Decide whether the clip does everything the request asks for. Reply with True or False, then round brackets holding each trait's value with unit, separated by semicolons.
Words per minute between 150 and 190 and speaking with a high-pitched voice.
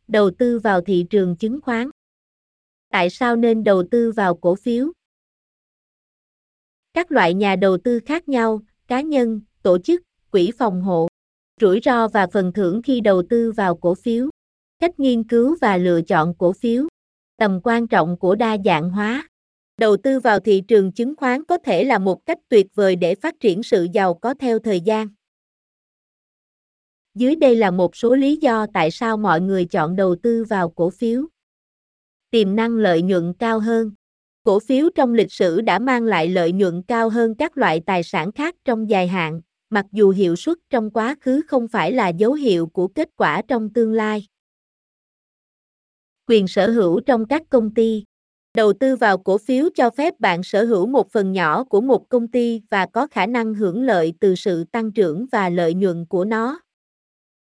True (185 wpm; 220 Hz)